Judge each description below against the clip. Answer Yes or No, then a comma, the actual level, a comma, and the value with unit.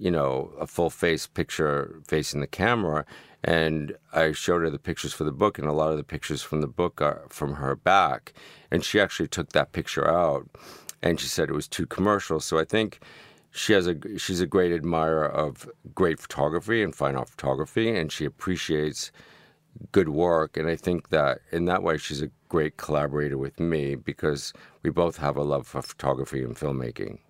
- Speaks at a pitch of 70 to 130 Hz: Yes, very low, 75 Hz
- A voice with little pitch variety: No, average, 3.1 semitones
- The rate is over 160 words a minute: Yes, average, 200 wpm